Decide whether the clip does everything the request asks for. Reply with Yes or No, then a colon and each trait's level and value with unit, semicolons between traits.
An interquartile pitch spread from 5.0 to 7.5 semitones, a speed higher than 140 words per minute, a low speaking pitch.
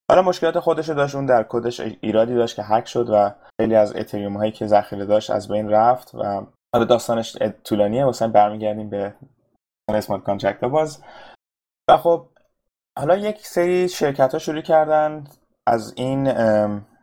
Yes: wide, 5.5 semitones; fast, 155 wpm; low, 115 Hz